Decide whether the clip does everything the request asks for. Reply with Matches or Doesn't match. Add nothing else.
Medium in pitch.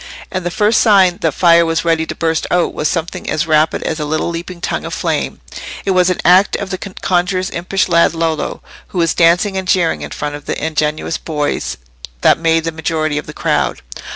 Matches